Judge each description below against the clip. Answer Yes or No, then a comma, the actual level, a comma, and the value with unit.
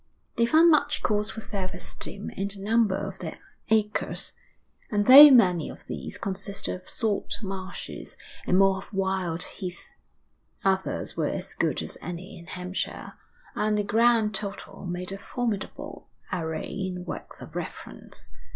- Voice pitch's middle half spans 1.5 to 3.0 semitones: Yes, narrow, 2.5 semitones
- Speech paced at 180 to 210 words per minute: No, average, 150 wpm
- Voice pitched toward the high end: Yes, high, 195 Hz